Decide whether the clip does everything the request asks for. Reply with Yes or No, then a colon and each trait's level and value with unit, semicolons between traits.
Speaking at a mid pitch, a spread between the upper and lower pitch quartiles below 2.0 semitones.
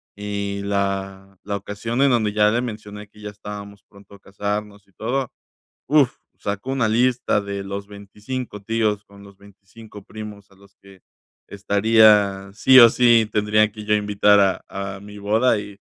No: low, 105 Hz; narrow, 1.5 semitones